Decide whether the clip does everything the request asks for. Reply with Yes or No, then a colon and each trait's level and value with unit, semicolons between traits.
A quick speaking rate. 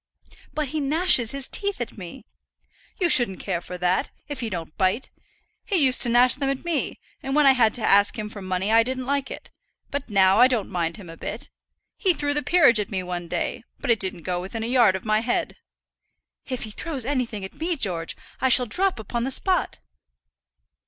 Yes: fast, 215 wpm